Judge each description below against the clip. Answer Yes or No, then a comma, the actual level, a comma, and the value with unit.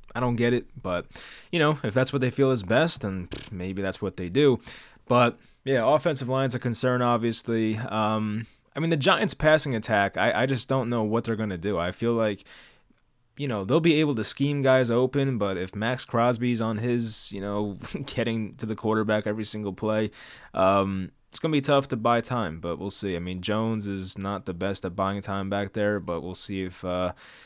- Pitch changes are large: No, average, 4.2 semitones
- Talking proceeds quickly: Yes, fast, 215 wpm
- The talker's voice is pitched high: No, low, 110 Hz